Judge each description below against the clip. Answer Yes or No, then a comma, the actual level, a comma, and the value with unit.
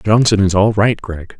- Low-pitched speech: Yes, low, 100 Hz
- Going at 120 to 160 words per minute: No, fast, 215 wpm